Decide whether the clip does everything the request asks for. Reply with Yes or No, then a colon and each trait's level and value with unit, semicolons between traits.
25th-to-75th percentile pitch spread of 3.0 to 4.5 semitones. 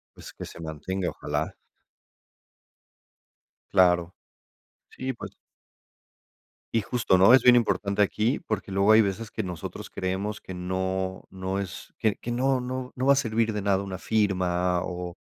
Yes: average, 3.4 semitones